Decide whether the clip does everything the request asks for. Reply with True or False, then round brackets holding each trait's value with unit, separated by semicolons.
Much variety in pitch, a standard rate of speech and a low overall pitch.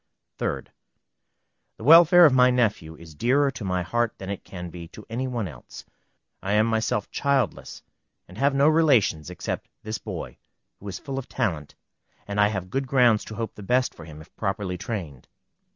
True (6.0 semitones; 185 wpm; 110 Hz)